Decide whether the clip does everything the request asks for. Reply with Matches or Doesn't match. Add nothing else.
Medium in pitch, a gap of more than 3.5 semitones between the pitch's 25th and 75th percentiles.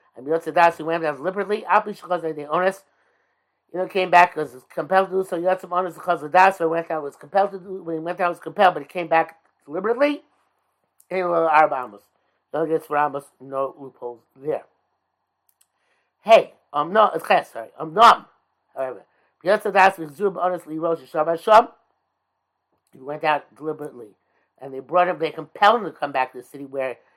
Matches